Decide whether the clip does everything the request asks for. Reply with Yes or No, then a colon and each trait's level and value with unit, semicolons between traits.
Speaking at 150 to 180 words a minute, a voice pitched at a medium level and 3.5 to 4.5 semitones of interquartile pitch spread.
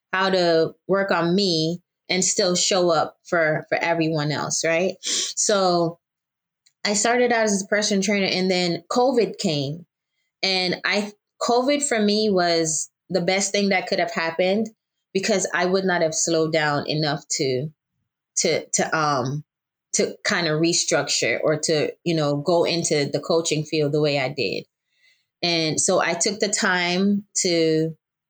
Yes: average, 160 wpm; medium, 175 Hz; average, 3.9 semitones